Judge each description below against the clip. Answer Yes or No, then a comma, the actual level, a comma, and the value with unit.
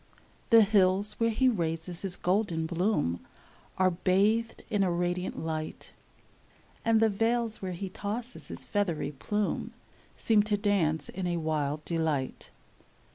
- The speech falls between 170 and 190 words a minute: No, slow, 135 wpm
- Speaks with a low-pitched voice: No, medium, 185 Hz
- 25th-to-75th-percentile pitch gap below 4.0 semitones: No, average, 4.4 semitones